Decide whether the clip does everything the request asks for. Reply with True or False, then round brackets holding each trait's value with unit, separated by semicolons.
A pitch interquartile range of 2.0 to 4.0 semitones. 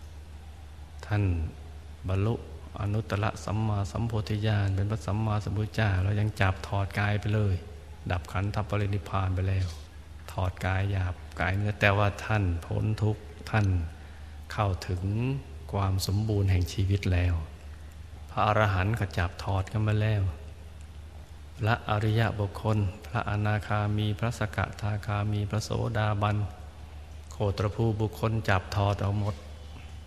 False (4.4 semitones)